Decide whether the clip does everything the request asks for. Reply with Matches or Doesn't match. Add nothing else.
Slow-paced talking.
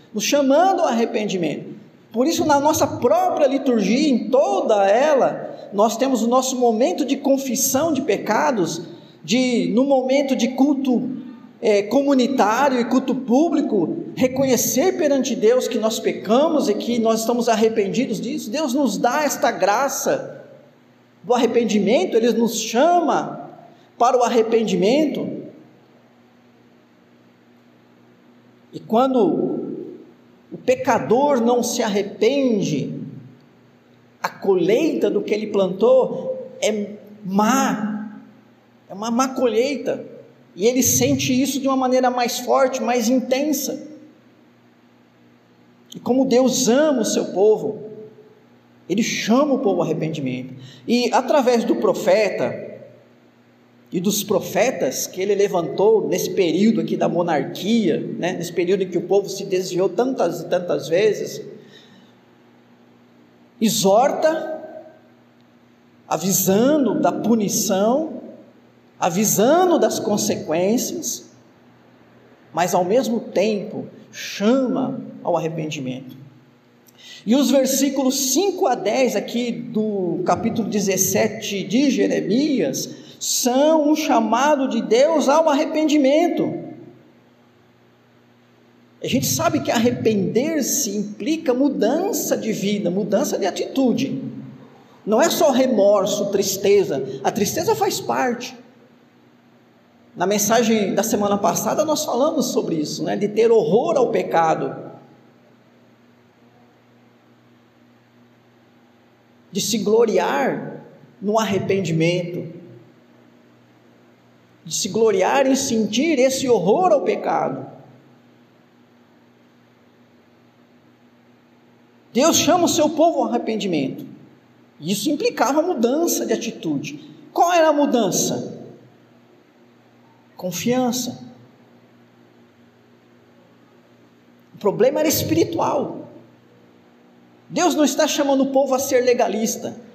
Matches